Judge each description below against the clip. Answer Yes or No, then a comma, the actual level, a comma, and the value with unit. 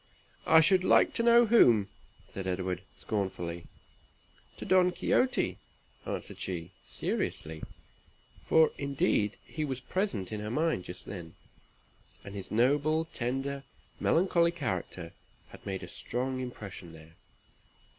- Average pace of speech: No, slow, 125 wpm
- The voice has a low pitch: Yes, low, 120 Hz